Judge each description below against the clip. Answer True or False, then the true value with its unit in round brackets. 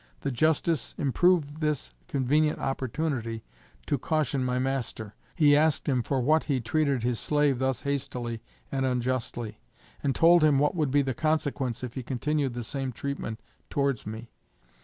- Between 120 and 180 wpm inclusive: True (160 wpm)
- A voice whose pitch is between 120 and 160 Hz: True (135 Hz)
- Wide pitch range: False (3.3 semitones)